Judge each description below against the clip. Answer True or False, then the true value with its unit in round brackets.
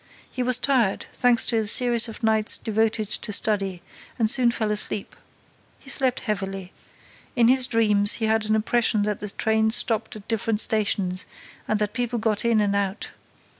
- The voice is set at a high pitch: True (220 Hz)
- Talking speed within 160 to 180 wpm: True (175 wpm)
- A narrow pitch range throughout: True (2.1 semitones)